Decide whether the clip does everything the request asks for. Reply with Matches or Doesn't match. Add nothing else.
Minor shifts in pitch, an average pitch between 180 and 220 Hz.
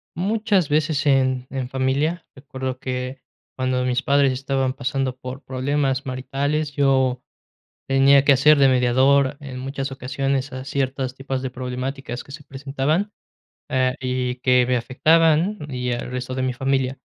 Doesn't match